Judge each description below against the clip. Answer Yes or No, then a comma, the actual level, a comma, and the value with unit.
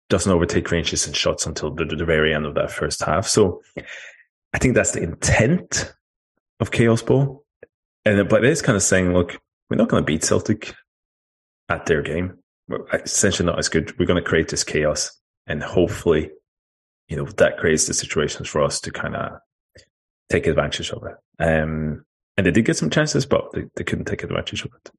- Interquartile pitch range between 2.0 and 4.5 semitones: Yes, average, 4.0 semitones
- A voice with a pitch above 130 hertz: No, very low, 85 Hz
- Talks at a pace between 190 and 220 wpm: Yes, average, 200 wpm